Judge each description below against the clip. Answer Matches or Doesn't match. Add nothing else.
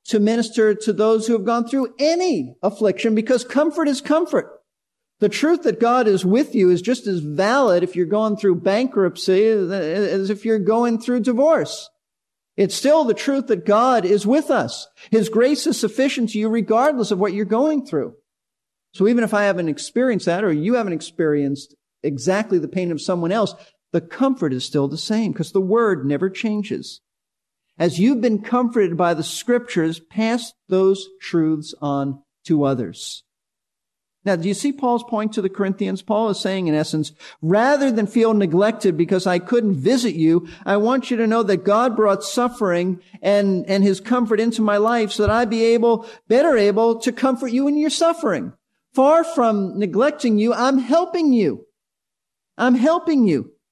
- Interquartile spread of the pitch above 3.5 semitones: Matches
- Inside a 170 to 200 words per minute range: Matches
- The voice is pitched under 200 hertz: Doesn't match